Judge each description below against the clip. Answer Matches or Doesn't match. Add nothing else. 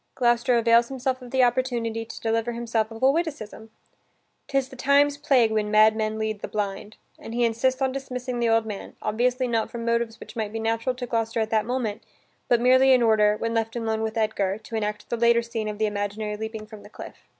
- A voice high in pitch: Matches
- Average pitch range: Doesn't match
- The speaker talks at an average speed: Doesn't match